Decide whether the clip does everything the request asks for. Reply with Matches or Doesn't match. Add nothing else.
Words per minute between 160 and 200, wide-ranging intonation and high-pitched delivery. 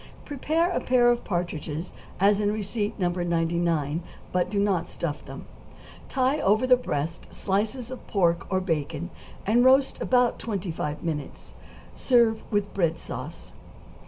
Doesn't match